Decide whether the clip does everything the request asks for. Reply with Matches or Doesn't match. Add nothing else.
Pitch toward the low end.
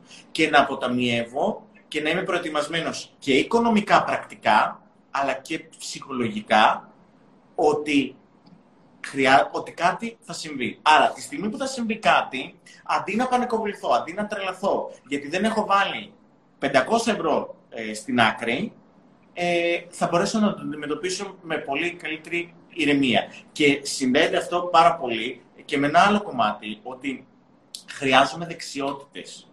Doesn't match